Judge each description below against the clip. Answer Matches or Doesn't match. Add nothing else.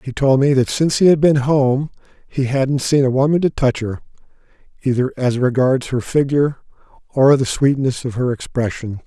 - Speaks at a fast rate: Doesn't match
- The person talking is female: Doesn't match